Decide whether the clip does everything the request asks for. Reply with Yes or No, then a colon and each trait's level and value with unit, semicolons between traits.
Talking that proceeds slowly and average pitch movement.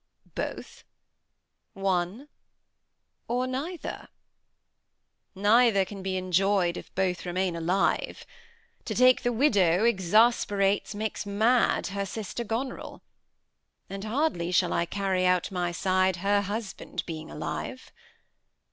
Yes: slow, 110 wpm; average, 3.6 semitones